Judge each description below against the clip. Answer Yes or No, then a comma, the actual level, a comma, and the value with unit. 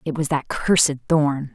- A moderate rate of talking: Yes, average, 195 wpm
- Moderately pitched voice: Yes, medium, 145 Hz